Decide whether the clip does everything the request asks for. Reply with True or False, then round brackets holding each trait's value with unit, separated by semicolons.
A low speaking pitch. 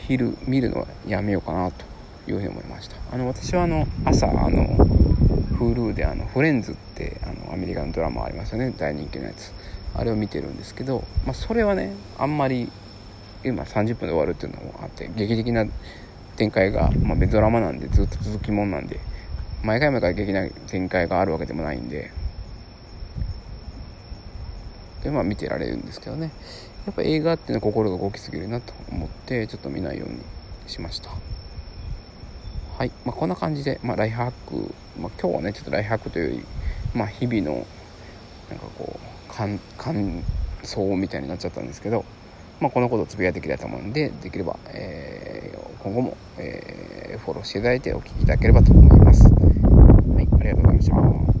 True (100 Hz)